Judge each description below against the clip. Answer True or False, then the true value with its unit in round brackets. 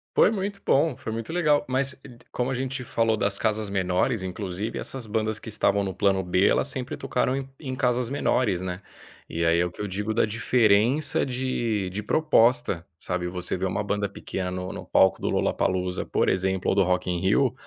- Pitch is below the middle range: True (105 Hz)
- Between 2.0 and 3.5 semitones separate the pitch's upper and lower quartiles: False (5.3 semitones)